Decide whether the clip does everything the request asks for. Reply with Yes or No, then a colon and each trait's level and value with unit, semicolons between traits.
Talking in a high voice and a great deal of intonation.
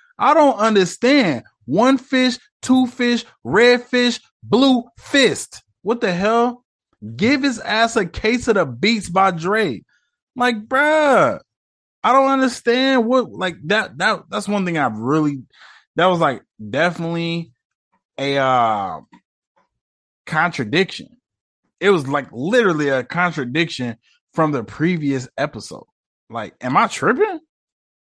Yes: high, 220 Hz; wide, 7.6 semitones